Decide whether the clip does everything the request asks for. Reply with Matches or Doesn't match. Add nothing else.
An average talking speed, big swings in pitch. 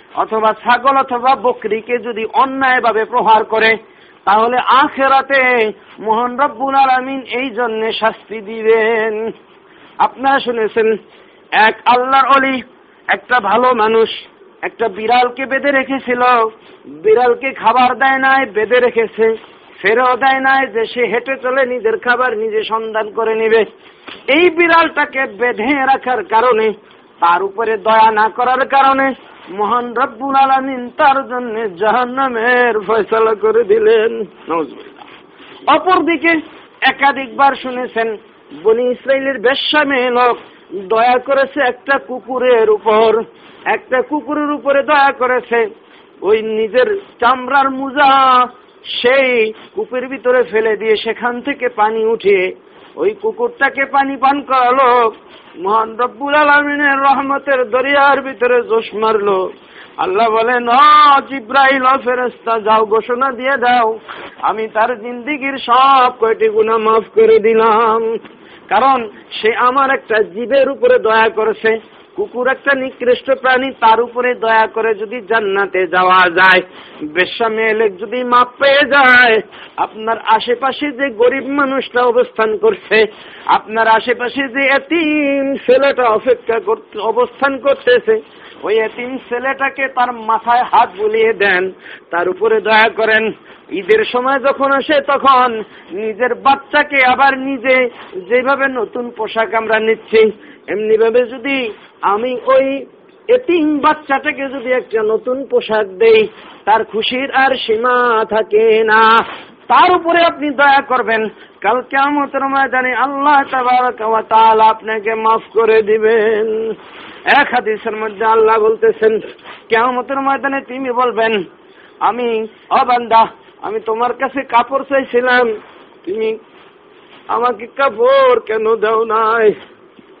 Doesn't match